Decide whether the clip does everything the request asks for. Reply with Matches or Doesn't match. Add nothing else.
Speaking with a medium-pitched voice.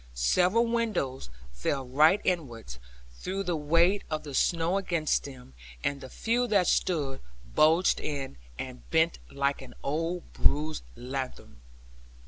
Matches